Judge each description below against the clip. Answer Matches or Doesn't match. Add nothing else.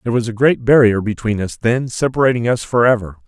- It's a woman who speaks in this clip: Doesn't match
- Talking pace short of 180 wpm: Doesn't match